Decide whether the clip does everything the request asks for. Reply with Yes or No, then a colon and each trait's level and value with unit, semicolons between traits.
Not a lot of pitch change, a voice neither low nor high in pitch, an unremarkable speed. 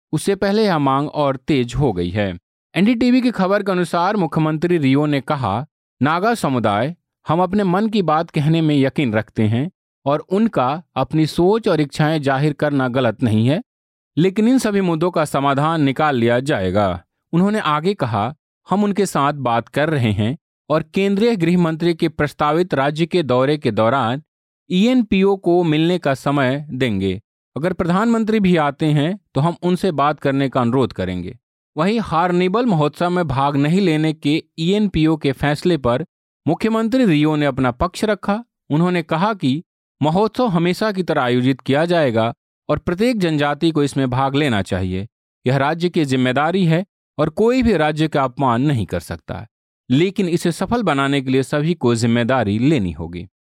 No: average, 5.3 semitones; medium, 155 Hz; average, 170 wpm